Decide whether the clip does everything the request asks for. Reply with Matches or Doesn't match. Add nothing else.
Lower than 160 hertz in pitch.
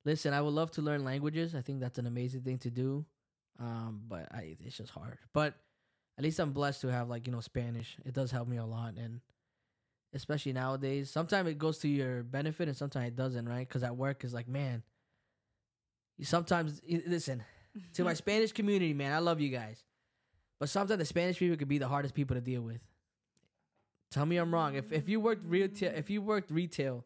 Matches